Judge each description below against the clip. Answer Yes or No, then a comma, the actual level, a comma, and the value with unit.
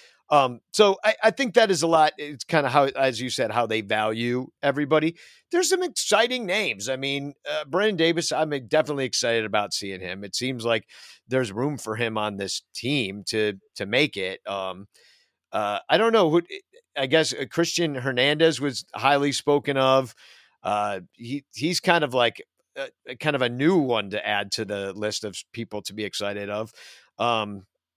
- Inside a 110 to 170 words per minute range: No, average, 185 wpm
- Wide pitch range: Yes, wide, 7.1 semitones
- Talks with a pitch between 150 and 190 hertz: No, low, 135 Hz